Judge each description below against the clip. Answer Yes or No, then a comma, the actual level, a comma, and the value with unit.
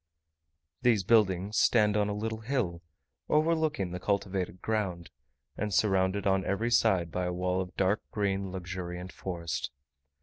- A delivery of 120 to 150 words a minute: Yes, average, 140 wpm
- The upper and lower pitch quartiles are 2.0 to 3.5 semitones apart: Yes, average, 2.8 semitones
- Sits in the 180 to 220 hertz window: No, very low, 95 Hz